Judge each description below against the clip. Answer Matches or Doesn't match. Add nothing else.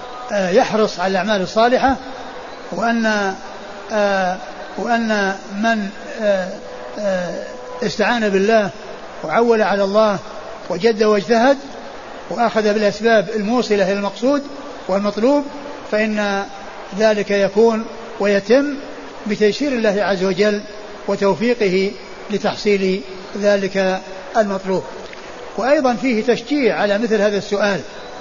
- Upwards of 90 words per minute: Doesn't match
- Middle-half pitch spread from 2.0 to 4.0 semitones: Matches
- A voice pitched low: Doesn't match